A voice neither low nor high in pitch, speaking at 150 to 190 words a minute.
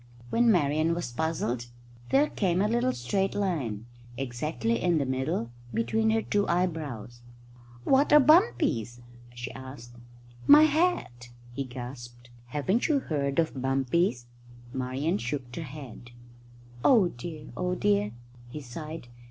No: medium, 145 Hz; slow, 135 wpm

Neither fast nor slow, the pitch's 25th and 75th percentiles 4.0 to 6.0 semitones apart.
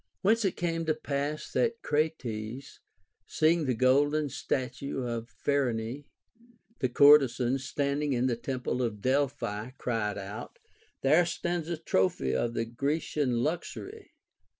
No: slow, 125 wpm; average, 4.3 semitones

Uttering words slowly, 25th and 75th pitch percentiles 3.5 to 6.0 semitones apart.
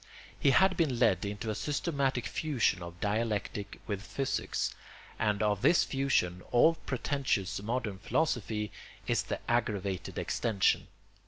Yes: slow, 130 wpm; average, 5.0 semitones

